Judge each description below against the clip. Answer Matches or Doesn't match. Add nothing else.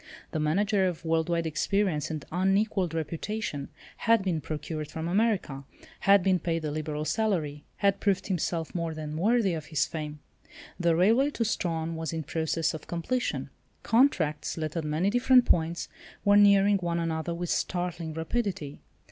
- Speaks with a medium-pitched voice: Matches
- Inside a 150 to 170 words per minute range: Matches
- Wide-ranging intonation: Doesn't match